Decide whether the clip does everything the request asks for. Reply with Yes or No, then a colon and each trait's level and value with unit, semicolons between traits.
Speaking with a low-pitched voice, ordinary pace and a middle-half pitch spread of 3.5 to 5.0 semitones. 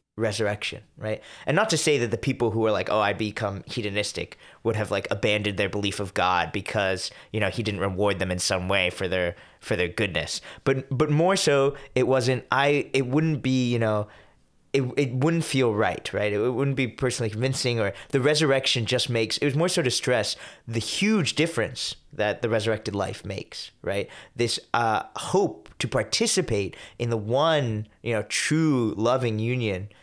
Yes: low, 120 Hz; average, 190 wpm; average, 4.6 semitones